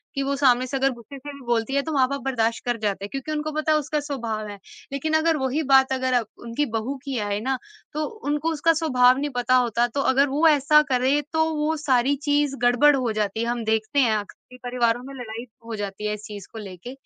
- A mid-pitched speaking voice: No, very high, 260 Hz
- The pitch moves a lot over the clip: No, average, 3.8 semitones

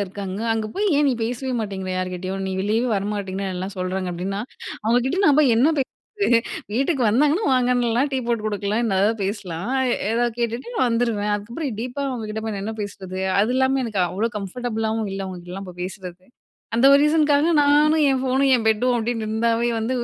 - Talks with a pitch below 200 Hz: No, high, 225 Hz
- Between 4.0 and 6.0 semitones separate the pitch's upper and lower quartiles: Yes, average, 4.5 semitones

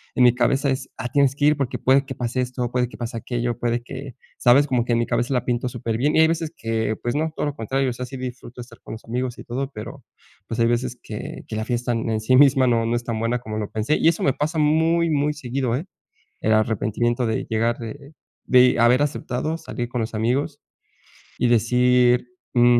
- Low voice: Yes, low, 125 Hz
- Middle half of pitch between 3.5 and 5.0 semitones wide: No, narrow, 2.5 semitones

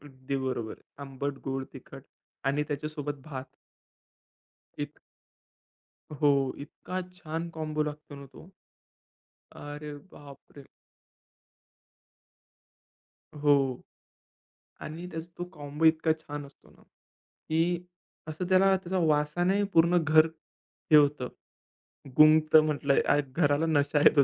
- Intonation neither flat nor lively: No, narrow, 2.1 semitones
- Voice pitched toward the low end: No, medium, 150 Hz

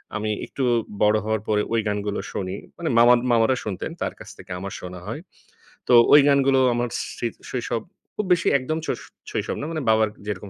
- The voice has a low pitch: Yes, low, 110 Hz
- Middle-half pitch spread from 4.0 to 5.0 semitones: Yes, average, 4.3 semitones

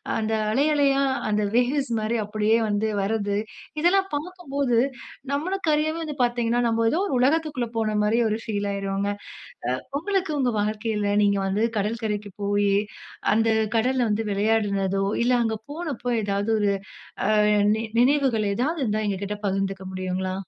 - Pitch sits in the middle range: No, high, 225 Hz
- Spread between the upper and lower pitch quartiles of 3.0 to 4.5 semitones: No, average, 5.0 semitones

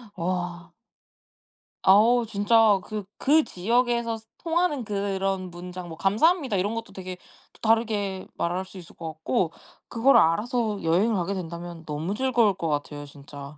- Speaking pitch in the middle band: No, high, 195 Hz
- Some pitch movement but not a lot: Yes, average, 4.8 semitones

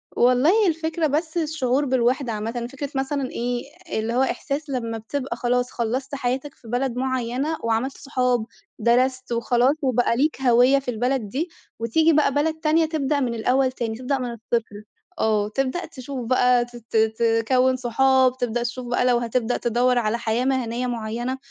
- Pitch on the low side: No, very high, 250 Hz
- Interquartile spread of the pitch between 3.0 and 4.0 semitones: No, narrow, 2.4 semitones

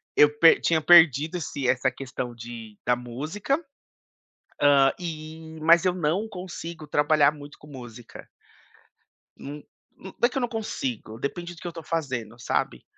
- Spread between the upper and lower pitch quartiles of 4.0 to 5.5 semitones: Yes, average, 4.9 semitones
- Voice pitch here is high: No, medium, 150 Hz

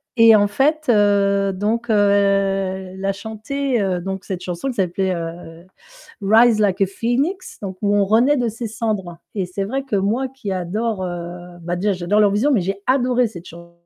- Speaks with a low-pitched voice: No, high, 200 Hz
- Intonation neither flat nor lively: Yes, average, 3.6 semitones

